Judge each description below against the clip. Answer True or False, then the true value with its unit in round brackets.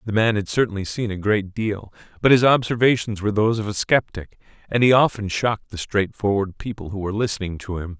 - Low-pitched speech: True (105 Hz)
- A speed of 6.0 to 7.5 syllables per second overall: True (6.1 syllables/s)